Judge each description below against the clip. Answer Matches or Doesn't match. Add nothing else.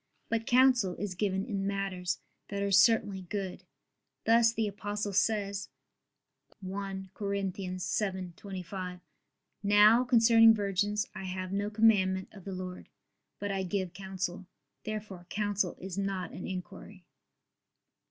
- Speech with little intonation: Matches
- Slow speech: Matches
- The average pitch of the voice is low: Doesn't match